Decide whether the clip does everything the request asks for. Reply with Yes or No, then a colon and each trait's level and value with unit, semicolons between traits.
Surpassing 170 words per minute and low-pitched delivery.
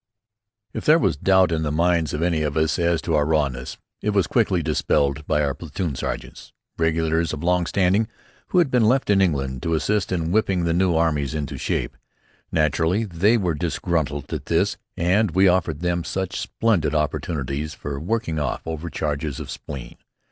Yes: average, 180 wpm; very low, 80 Hz